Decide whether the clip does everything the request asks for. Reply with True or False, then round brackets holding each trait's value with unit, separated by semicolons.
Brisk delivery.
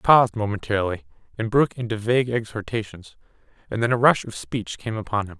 False (190 wpm)